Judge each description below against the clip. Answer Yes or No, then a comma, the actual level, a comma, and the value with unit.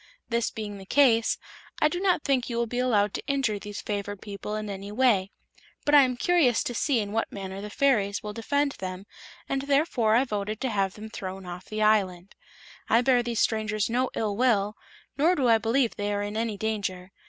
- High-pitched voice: Yes, high, 220 Hz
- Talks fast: Yes, fast, 210 wpm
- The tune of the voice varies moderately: Yes, average, 3.7 semitones